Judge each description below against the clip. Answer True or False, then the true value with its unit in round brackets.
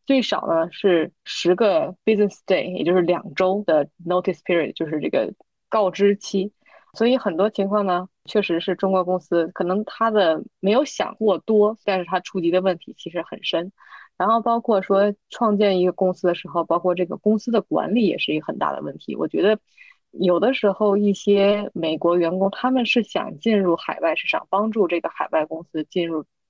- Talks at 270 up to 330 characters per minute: True (320 characters per minute)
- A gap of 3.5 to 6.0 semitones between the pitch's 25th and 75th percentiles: False (3.1 semitones)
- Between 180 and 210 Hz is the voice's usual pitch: True (190 Hz)